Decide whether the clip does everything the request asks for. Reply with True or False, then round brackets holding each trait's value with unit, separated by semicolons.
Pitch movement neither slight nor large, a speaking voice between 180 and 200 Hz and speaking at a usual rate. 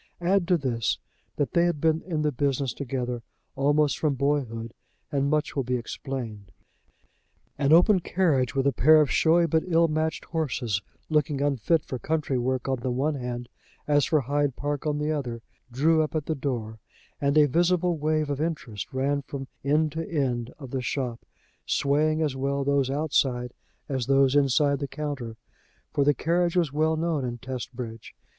False (3.3 semitones; 140 Hz; 180 wpm)